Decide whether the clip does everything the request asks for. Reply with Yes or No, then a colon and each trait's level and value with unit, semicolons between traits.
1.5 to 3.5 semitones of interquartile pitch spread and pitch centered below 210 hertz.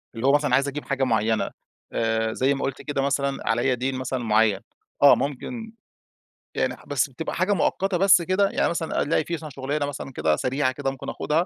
Yes: average, 3.2 semitones; medium, 140 Hz